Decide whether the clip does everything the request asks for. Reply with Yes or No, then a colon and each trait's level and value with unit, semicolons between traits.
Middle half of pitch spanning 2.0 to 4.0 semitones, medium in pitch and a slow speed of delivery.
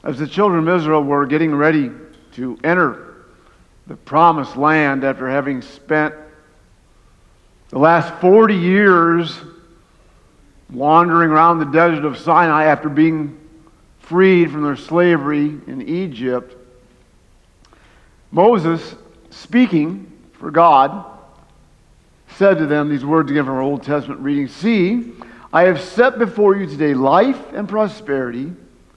Yes: average, 3.6 semitones; medium, 155 Hz; slow, 120 wpm